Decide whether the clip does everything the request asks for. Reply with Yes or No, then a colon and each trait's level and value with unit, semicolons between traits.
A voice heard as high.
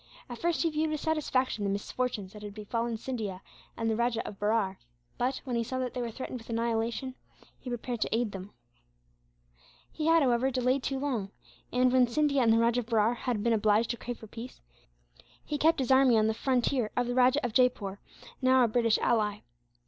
Yes: high, 240 Hz